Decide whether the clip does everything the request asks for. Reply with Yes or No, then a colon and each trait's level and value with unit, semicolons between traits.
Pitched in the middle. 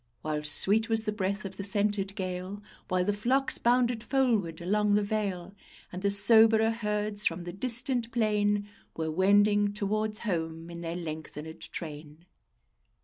No: high, 205 Hz